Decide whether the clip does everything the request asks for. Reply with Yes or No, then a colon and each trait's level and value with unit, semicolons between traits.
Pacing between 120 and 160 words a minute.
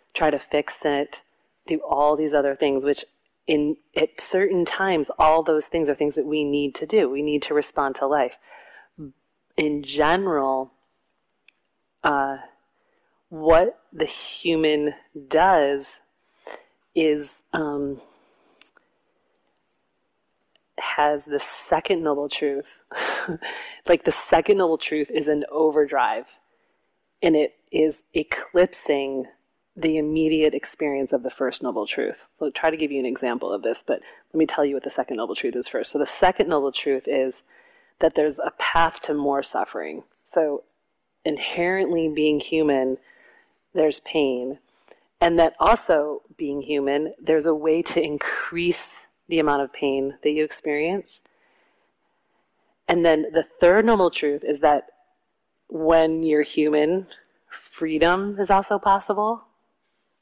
Yes: slow, 135 wpm